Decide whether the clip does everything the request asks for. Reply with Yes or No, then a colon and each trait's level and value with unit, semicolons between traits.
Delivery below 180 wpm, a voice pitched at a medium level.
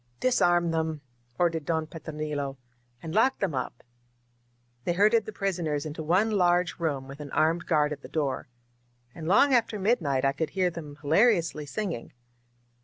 Yes: average, 170 wpm; medium, 160 Hz